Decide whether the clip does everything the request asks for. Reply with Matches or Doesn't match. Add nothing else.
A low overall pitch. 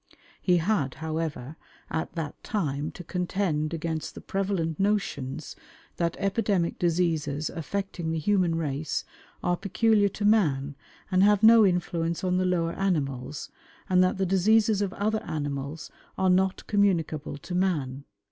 Doesn't match